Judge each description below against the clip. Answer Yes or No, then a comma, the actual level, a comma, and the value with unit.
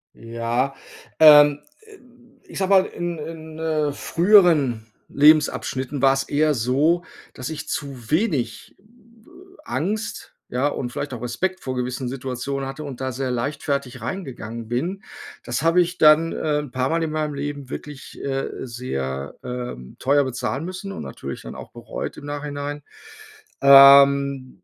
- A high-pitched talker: No, medium, 140 Hz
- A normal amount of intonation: Yes, average, 3.7 semitones